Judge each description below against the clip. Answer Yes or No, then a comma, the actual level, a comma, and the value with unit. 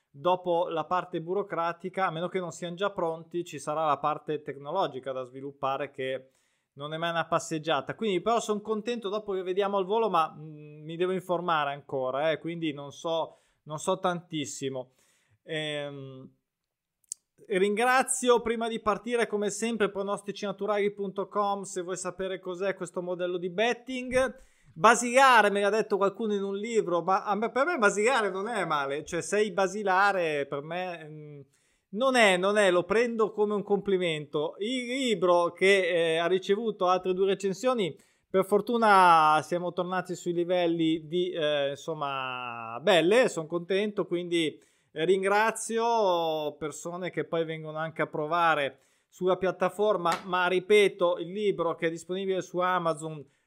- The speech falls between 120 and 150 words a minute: Yes, average, 145 wpm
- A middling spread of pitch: Yes, average, 4.1 semitones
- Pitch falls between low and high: Yes, medium, 180 Hz